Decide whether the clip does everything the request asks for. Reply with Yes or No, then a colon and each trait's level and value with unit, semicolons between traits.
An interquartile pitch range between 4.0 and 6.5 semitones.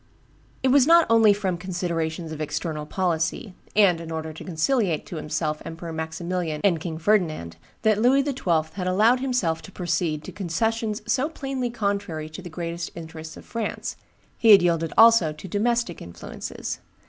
Yes: wide, 5.6 semitones